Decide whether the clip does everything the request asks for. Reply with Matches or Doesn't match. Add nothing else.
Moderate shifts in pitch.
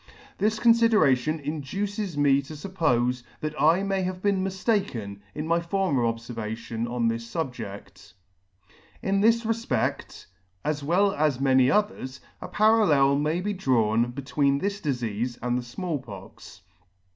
Doesn't match